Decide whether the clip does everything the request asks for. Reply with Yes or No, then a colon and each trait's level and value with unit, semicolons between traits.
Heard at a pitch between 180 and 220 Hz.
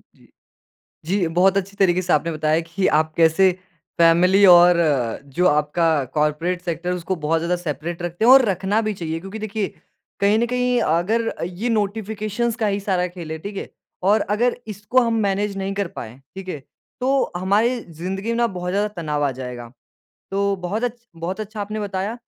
Yes: high, 190 Hz